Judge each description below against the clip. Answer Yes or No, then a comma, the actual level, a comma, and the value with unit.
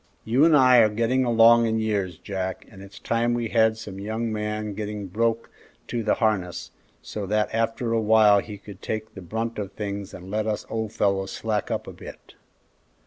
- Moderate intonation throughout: No, narrow, 2.0 semitones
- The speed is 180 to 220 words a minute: Yes, average, 200 wpm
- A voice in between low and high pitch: No, low, 110 Hz